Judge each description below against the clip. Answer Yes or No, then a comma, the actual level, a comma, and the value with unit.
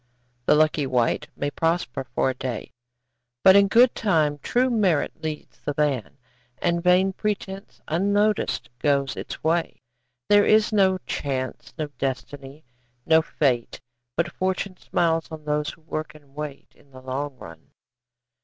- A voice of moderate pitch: Yes, medium, 155 Hz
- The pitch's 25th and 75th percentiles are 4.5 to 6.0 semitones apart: Yes, average, 5.2 semitones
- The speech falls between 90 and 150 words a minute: Yes, average, 145 wpm